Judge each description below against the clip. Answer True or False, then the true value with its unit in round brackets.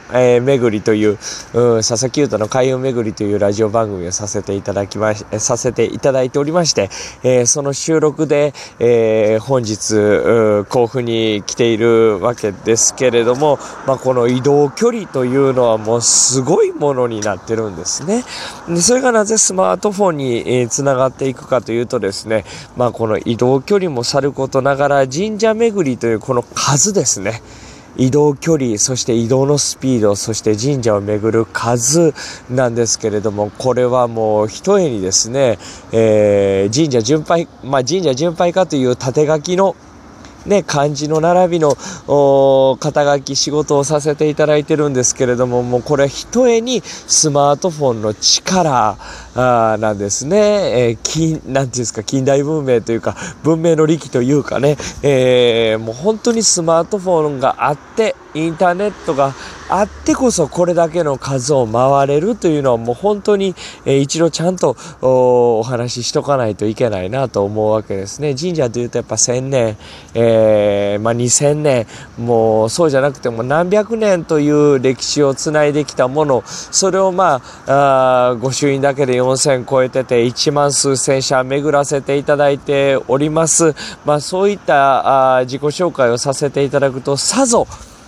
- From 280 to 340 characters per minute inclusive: True (330 characters per minute)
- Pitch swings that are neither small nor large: True (4.7 semitones)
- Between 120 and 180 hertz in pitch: True (135 Hz)